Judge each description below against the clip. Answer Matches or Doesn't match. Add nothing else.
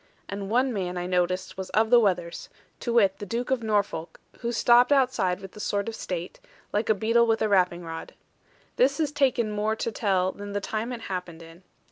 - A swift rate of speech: Matches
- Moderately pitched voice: Doesn't match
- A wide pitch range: Doesn't match